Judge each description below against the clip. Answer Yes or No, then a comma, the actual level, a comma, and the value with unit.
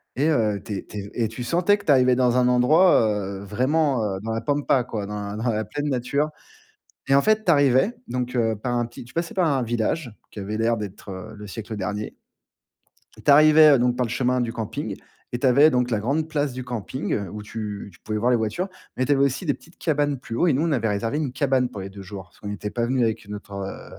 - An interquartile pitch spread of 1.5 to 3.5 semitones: No, average, 4.9 semitones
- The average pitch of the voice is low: Yes, low, 125 Hz